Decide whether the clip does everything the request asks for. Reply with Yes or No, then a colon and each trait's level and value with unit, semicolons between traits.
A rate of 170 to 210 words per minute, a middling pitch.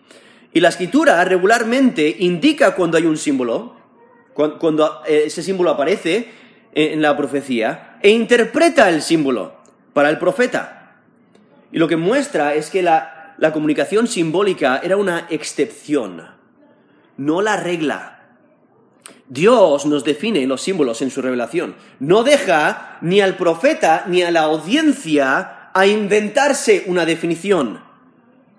No: slow, 125 wpm; medium, 170 Hz